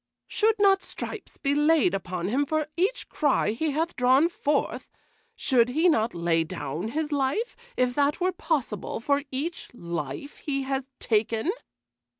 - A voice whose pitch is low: No, very high, 275 Hz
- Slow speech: No, average, 155 wpm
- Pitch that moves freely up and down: Yes, wide, 6.0 semitones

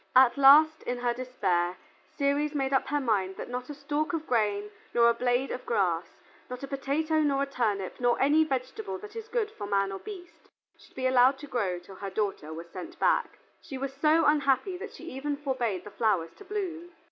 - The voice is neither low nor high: No, very high, 265 Hz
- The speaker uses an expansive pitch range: Yes, wide, 5.7 semitones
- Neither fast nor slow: No, fast, 210 wpm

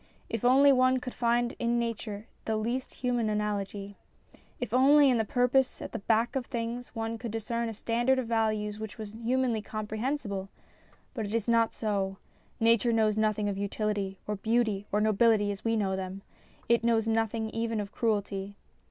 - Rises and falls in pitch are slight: Yes, narrow, 2.2 semitones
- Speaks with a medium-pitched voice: No, high, 225 Hz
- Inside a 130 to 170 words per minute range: No, average, 180 wpm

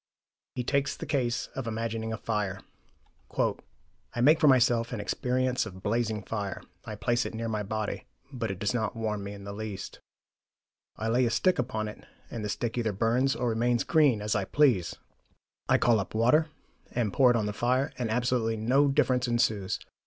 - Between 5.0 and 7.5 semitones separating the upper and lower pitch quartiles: No, average, 2.7 semitones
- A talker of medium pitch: No, low, 115 Hz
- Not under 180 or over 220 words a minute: Yes, average, 190 wpm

